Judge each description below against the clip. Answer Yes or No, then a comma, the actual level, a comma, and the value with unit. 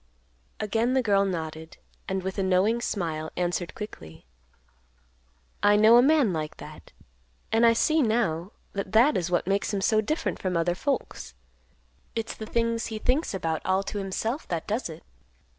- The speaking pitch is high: Yes, high, 200 Hz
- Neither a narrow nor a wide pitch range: Yes, average, 4.6 semitones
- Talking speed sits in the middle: Yes, average, 170 wpm